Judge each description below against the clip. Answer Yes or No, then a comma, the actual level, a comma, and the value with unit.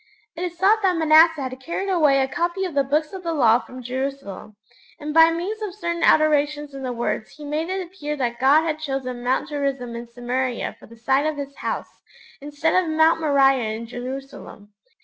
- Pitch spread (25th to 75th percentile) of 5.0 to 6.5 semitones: No, average, 4.1 semitones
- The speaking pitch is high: Yes, very high, 290 Hz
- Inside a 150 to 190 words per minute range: No, fast, 205 wpm